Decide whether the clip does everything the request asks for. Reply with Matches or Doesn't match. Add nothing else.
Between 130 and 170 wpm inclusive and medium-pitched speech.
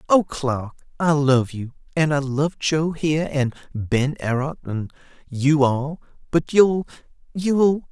Matches